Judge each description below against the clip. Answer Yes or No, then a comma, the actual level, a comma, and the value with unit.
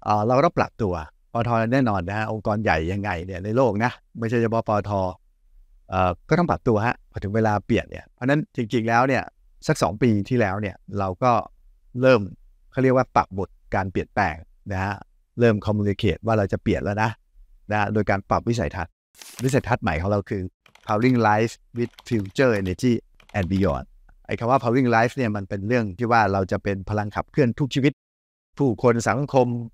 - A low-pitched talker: Yes, low, 105 Hz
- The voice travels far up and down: No, average, 3.8 semitones